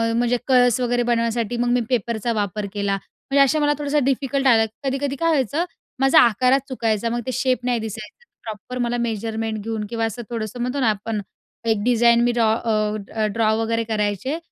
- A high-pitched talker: Yes, high, 235 Hz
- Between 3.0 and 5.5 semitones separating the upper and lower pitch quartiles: No, narrow, 2.6 semitones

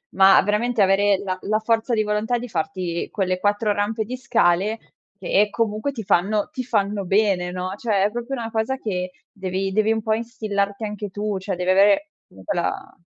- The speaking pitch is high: Yes, high, 205 Hz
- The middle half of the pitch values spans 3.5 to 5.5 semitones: No, narrow, 2.6 semitones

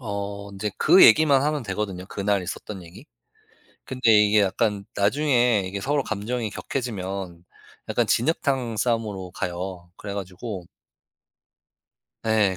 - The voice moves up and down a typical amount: Yes, average, 3.7 semitones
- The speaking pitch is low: Yes, low, 105 Hz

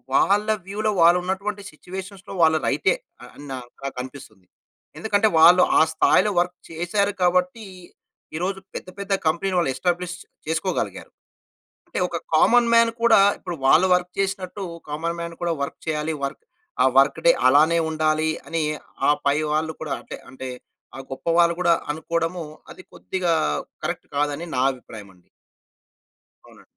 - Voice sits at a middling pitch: Yes, medium, 170 Hz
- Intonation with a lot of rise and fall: No, average, 3.6 semitones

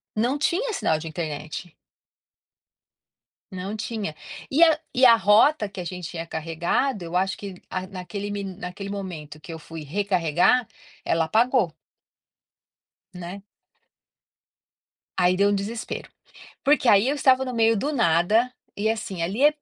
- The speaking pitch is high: Yes, high, 200 Hz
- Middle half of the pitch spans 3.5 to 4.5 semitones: No, average, 5.2 semitones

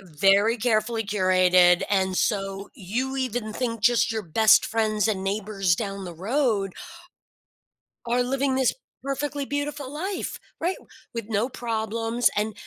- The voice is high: Yes, high, 220 Hz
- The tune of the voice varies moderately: Yes, average, 4.2 semitones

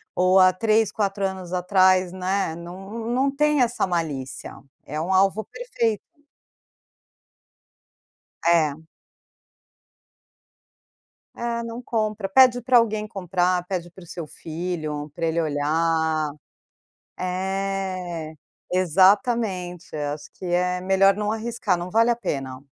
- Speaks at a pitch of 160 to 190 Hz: Yes, medium, 185 Hz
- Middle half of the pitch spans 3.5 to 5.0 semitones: Yes, average, 4.0 semitones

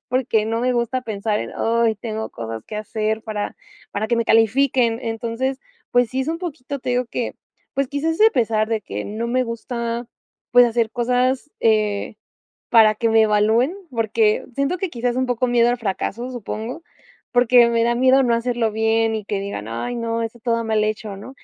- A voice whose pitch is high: Yes, high, 230 Hz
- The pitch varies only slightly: Yes, narrow, 2.2 semitones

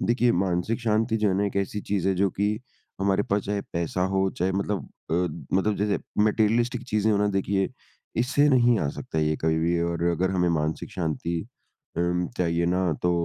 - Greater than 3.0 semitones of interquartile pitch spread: Yes, average, 3.5 semitones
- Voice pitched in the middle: No, very low, 95 Hz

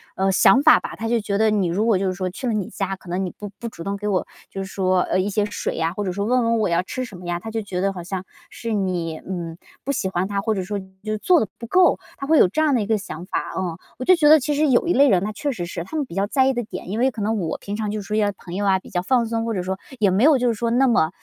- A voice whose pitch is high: Yes, high, 205 Hz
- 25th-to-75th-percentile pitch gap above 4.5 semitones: No, average, 4.0 semitones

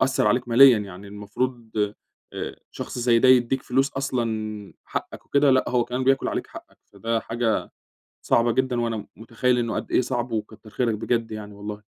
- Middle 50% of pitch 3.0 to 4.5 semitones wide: No, narrow, 2.6 semitones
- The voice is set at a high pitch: No, low, 120 Hz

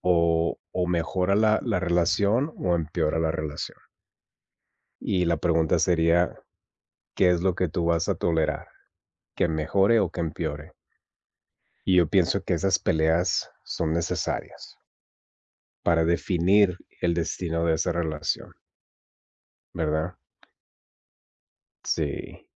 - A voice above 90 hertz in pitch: No, very low, 85 Hz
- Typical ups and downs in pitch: No, narrow, 2.0 semitones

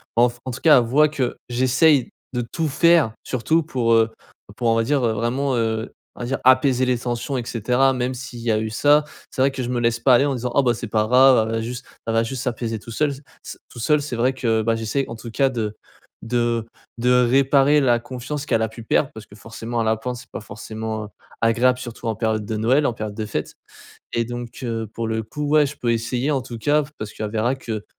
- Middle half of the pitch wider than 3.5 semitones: No, average, 2.8 semitones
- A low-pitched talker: Yes, low, 120 Hz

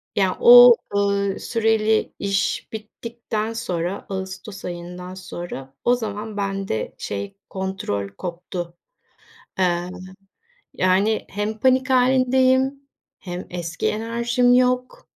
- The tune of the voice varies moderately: Yes, average, 4.7 semitones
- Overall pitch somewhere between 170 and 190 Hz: No, high, 200 Hz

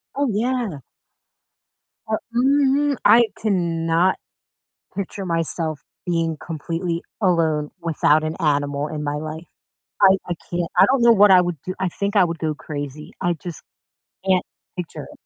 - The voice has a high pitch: No, medium, 170 Hz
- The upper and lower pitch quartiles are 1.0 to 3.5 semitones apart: No, average, 4.1 semitones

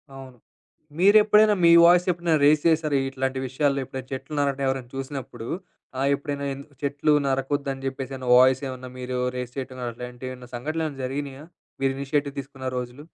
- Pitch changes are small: Yes, narrow, 2.0 semitones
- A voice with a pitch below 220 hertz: Yes, low, 135 Hz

